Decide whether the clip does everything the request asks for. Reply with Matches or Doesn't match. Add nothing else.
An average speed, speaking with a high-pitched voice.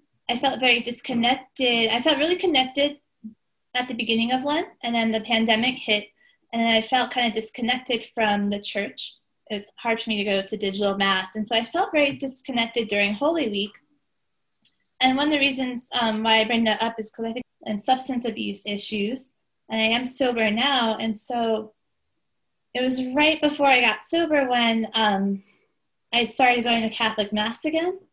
Matches